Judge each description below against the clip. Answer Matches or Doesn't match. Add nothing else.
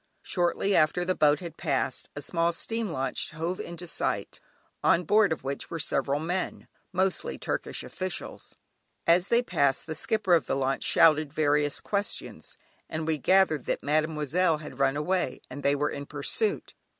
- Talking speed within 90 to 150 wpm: Doesn't match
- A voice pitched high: Doesn't match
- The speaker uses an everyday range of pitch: Matches